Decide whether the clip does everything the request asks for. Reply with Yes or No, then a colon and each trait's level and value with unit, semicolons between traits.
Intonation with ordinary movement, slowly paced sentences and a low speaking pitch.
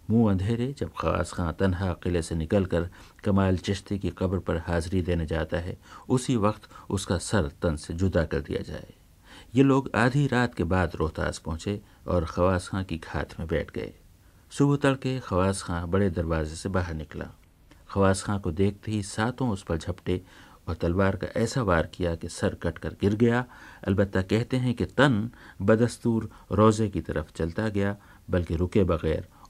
No: average, 3.8 semitones; average, 180 wpm; very low, 95 Hz